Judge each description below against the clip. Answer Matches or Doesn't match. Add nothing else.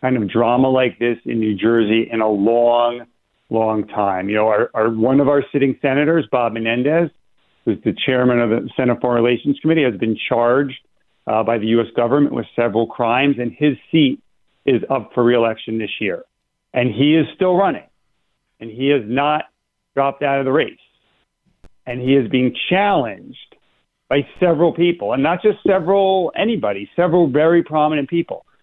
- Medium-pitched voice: Doesn't match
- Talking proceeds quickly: Doesn't match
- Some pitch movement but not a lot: Matches